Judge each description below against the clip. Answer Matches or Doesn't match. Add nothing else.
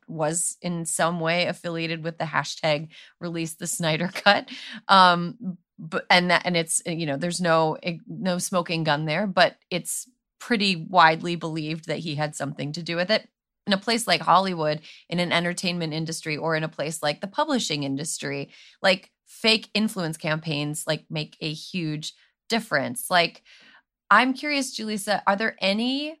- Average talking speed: Matches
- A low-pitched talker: Doesn't match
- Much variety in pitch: Doesn't match